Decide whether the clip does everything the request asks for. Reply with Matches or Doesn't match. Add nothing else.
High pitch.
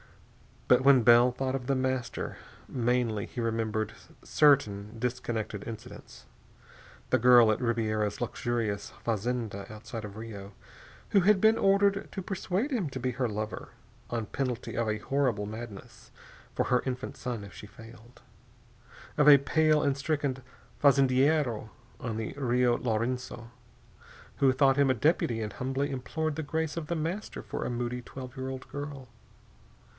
Doesn't match